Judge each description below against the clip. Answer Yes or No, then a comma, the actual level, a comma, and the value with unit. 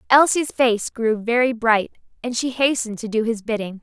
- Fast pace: No, average, 190 wpm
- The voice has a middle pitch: No, high, 230 Hz